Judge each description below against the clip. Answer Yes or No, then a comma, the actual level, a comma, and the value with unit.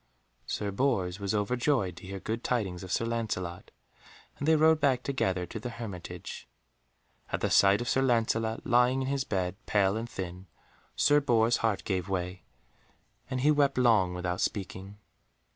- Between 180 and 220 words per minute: No, average, 165 wpm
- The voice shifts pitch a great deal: No, average, 4.9 semitones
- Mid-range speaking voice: No, low, 110 Hz